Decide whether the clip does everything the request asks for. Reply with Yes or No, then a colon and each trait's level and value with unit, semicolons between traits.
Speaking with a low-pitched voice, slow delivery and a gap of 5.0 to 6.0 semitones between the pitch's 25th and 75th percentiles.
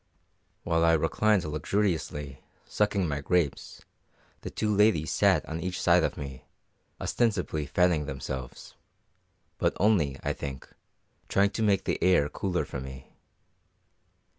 Yes: very low, 80 Hz; slow, 130 wpm; wide, 5.4 semitones